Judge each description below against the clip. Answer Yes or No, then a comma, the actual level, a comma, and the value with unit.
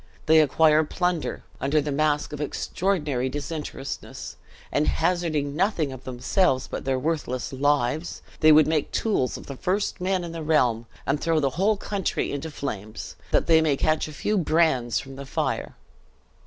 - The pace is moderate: Yes, average, 170 wpm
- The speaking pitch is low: No, medium, 150 Hz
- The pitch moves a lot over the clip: No, average, 3.3 semitones